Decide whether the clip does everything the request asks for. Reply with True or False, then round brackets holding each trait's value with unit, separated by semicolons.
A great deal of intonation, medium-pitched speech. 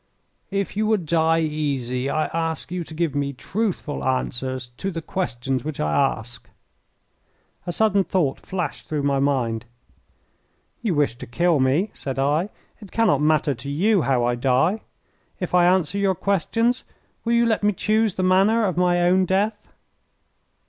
True (6.0 semitones; 165 Hz)